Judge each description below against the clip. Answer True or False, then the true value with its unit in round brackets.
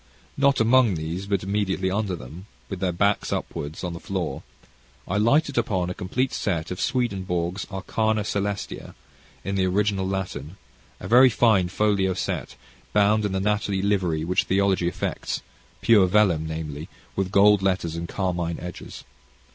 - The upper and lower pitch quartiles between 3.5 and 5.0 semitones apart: False (2.7 semitones)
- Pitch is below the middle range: True (95 Hz)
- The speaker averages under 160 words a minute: True (150 wpm)